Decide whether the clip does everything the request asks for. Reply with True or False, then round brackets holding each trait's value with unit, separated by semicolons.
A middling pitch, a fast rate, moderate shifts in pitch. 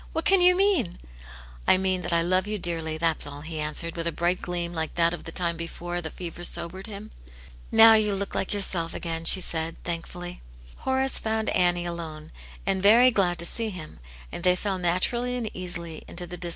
True (175 Hz; 220 wpm; 3.2 semitones)